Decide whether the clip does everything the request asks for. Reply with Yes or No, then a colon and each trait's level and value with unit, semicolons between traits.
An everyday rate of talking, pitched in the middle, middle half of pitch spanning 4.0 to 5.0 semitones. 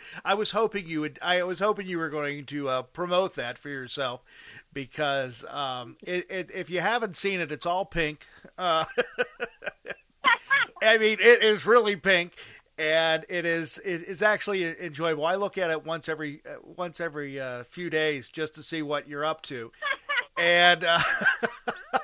Yes: average, 165 wpm; medium, 170 Hz; average, 4.3 semitones